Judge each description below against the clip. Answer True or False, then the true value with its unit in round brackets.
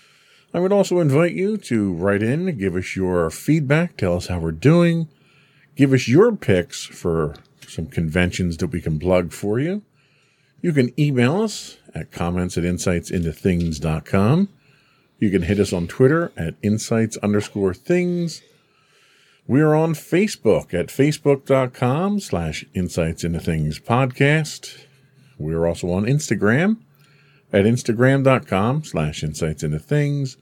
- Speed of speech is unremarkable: False (130 wpm)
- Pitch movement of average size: False (8.6 semitones)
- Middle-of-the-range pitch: False (125 Hz)